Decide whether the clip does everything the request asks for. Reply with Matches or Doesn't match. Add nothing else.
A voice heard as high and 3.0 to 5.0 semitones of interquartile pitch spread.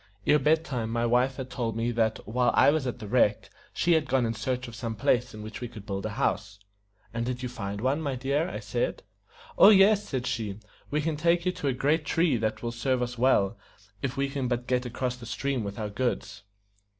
Doesn't match